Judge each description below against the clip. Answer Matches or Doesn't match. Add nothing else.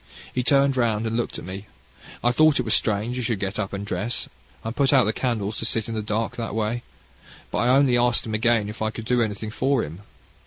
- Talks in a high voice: Doesn't match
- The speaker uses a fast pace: Matches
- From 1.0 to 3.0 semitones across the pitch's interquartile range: Matches